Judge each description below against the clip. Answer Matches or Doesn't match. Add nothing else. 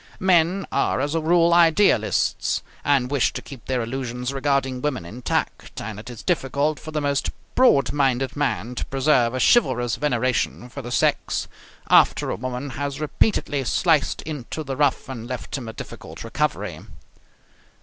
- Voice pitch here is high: Doesn't match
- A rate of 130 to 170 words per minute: Matches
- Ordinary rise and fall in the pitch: Matches